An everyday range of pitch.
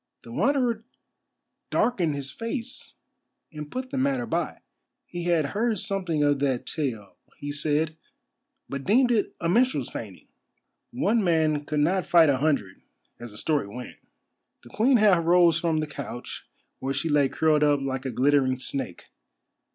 No: wide, 6.7 semitones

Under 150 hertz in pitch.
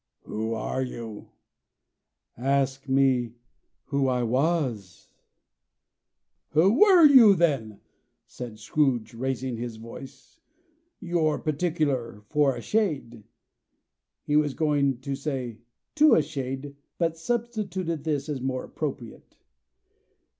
Yes: low, 135 Hz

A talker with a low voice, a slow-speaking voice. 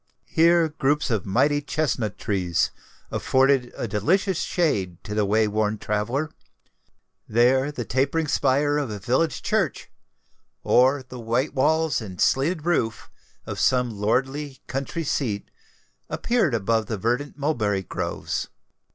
Yes: low, 130 Hz; slow, 130 wpm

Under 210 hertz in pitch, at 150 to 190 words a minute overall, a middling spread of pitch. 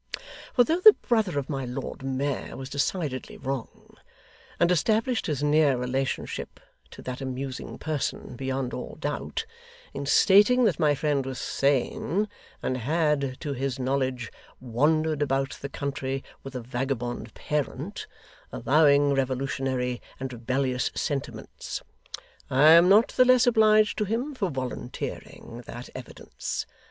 No: medium, 140 Hz; slow, 135 wpm; average, 3.7 semitones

